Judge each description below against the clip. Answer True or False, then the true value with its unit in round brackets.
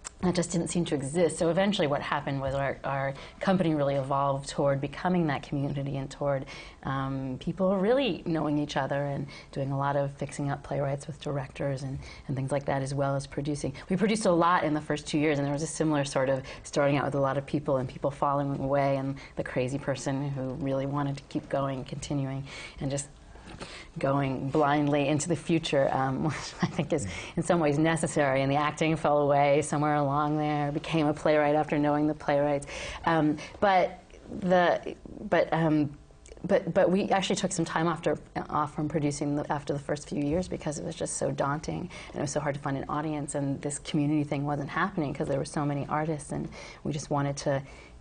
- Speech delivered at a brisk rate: True (215 wpm)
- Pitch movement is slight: True (2.3 semitones)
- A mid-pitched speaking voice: True (145 Hz)